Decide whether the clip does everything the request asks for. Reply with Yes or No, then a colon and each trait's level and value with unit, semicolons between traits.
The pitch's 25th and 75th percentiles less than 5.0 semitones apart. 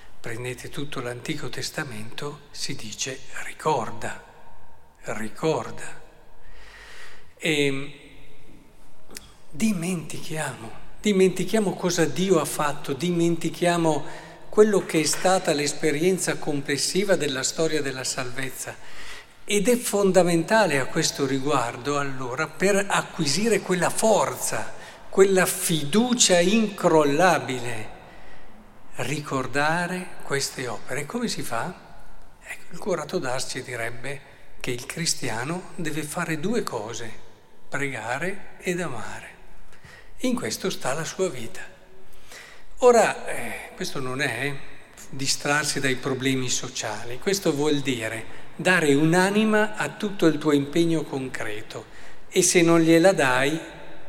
No: average, 5.3 semitones